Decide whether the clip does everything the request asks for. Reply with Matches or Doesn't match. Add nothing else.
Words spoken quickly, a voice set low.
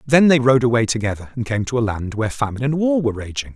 Matches